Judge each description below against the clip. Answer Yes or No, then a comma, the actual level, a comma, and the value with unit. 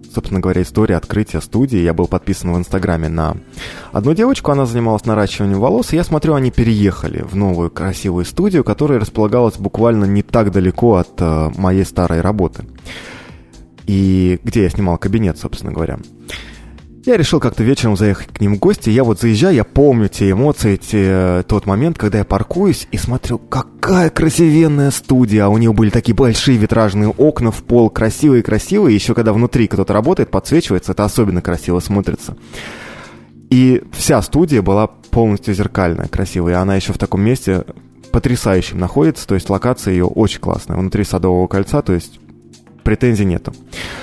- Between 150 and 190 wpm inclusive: Yes, fast, 160 wpm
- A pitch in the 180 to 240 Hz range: No, low, 105 Hz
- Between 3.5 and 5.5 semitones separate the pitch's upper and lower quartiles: Yes, average, 4.4 semitones